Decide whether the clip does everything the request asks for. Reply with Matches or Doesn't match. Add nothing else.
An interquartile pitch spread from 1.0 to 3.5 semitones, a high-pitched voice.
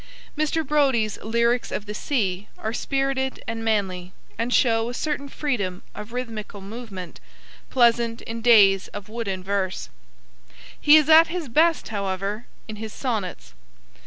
Doesn't match